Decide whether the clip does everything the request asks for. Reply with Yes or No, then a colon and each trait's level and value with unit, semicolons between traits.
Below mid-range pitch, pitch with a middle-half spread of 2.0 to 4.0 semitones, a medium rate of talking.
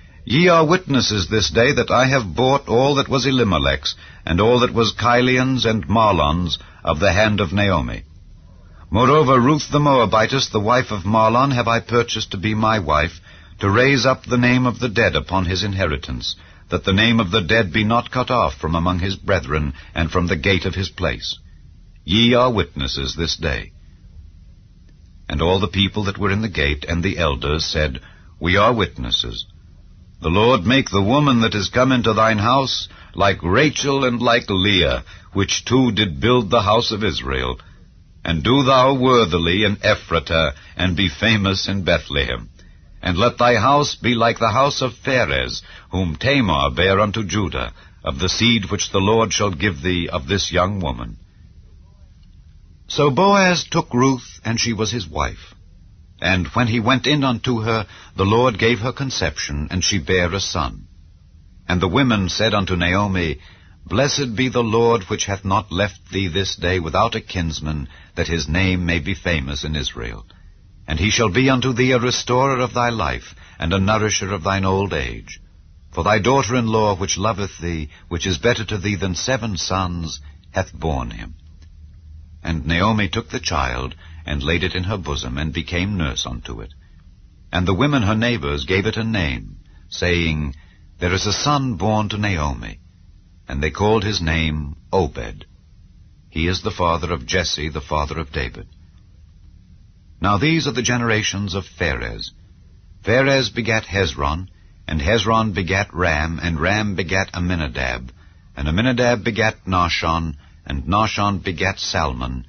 No: very low, 95 Hz; average, 5.1 semitones; average, 170 wpm